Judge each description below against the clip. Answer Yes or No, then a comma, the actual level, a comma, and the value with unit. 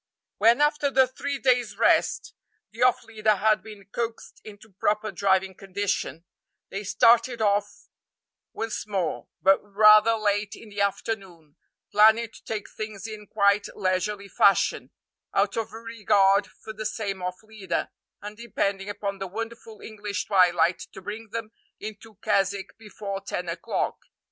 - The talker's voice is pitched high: Yes, high, 210 Hz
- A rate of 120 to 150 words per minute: Yes, average, 145 wpm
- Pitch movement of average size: No, narrow, 2.1 semitones